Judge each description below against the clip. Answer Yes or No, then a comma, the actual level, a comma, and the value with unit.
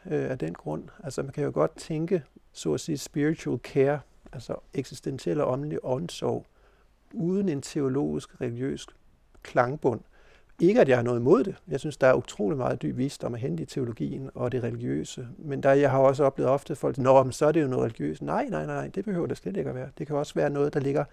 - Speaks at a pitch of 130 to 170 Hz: Yes, low, 135 Hz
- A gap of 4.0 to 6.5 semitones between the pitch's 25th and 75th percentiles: No, narrow, 2.6 semitones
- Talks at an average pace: No, fast, 230 wpm